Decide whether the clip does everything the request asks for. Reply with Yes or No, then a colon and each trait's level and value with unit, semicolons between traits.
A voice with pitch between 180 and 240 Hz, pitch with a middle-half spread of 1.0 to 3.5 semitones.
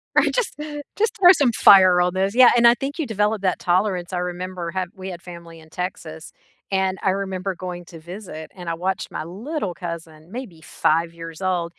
Yes: medium, 185 Hz; average, 2.7 semitones